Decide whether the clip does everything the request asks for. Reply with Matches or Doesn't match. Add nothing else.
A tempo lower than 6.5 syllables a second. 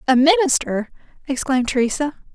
Matches